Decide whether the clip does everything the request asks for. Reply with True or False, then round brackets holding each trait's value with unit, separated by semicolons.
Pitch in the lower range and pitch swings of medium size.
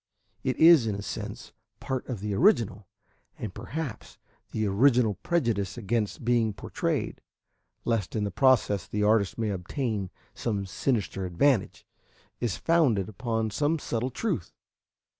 True (110 Hz; 4.3 semitones)